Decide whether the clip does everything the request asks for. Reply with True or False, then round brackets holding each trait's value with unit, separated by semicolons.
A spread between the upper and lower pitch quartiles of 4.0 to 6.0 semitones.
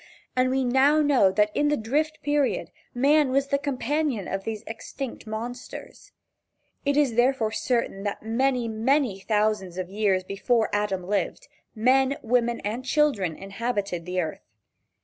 True (4.8 semitones)